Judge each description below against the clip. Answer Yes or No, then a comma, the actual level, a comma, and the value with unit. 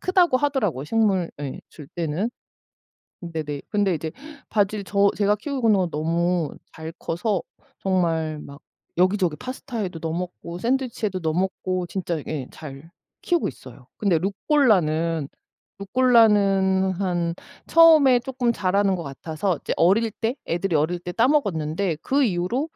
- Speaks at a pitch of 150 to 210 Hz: Yes, medium, 185 Hz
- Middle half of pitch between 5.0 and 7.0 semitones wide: Yes, average, 5.3 semitones